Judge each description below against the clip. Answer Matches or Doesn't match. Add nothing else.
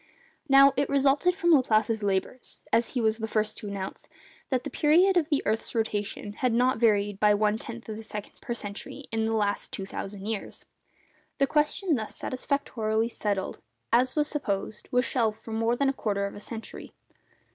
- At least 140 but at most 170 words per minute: Doesn't match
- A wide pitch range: Doesn't match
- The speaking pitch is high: Matches